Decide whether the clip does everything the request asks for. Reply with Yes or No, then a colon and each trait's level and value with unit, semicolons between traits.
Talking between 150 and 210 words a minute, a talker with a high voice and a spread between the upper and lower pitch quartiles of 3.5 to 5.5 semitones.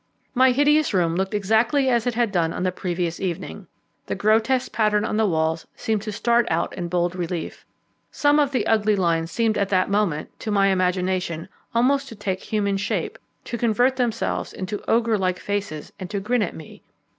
Yes: average, 190 wpm; high, 205 Hz; average, 4.3 semitones